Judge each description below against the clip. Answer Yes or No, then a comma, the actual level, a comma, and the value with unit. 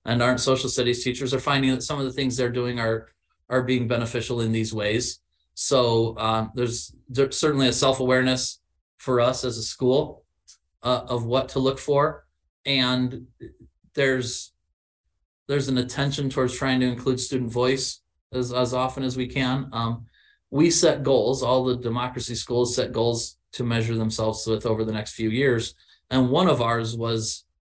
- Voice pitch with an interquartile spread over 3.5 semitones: No, narrow, 2.4 semitones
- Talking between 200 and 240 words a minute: No, average, 175 wpm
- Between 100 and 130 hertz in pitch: Yes, low, 125 Hz